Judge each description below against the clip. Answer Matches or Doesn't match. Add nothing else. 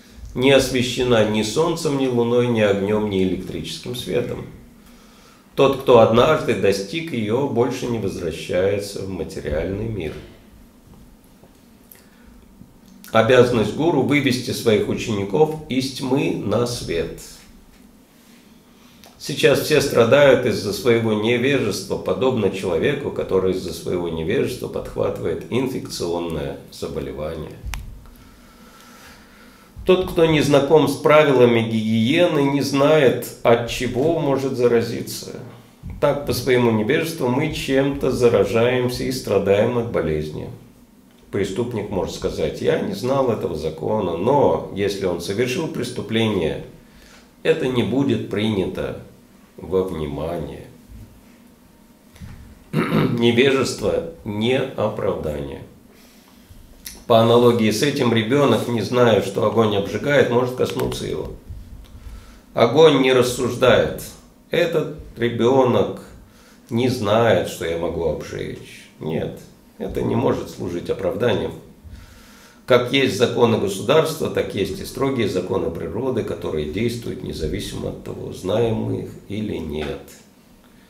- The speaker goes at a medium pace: Doesn't match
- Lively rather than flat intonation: Doesn't match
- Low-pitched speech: Matches